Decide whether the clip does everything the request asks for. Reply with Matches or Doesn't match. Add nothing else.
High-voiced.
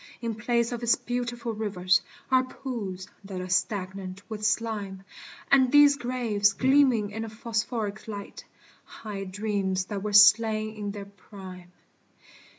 Matches